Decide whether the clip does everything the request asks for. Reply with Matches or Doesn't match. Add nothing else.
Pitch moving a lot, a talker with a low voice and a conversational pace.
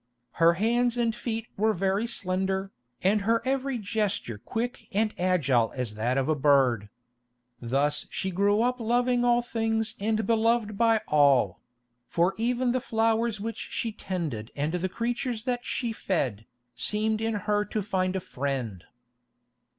Doesn't match